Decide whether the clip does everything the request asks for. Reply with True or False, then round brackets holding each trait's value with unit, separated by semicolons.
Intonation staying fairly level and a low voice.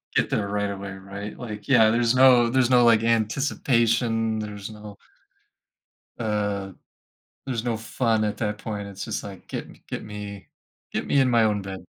True (2.3 semitones; 110 Hz)